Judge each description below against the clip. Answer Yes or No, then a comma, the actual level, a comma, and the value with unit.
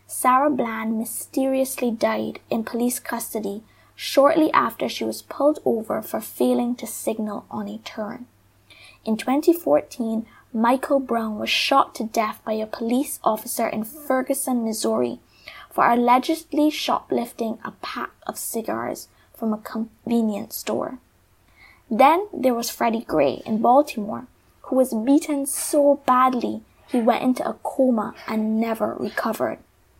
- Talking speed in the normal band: No, slow, 130 wpm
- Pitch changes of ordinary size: Yes, average, 3.8 semitones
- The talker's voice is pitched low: No, high, 240 Hz